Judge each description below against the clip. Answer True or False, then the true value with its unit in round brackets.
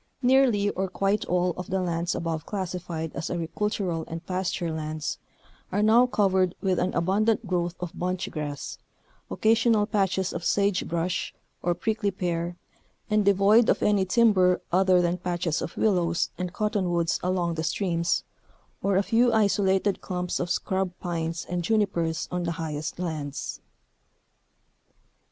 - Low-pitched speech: False (180 Hz)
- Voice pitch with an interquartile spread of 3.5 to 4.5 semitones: False (2.9 semitones)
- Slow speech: False (145 wpm)